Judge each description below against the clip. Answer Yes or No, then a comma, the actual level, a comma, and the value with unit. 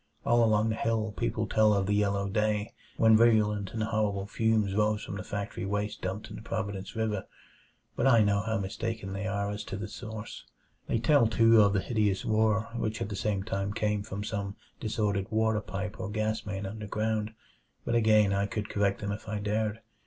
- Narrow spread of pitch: Yes, narrow, 1.5 semitones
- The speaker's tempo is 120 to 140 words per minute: No, average, 200 wpm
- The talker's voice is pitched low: Yes, low, 105 Hz